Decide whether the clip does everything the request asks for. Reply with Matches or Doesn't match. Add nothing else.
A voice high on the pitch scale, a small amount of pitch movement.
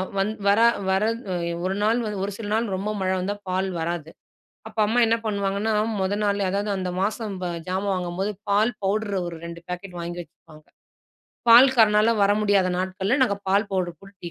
Matches